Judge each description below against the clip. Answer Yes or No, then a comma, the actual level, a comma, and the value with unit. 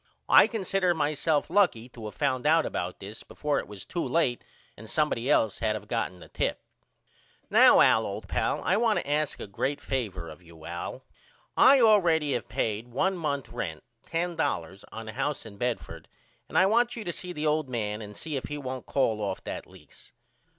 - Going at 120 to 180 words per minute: No, average, 200 wpm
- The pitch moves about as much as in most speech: No, wide, 7.4 semitones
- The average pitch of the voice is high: No, low, 135 Hz